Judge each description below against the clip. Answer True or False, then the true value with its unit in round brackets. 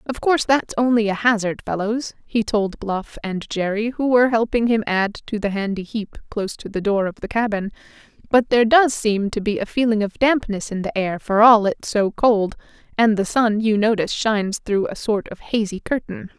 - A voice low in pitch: False (215 Hz)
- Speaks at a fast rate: True (210 wpm)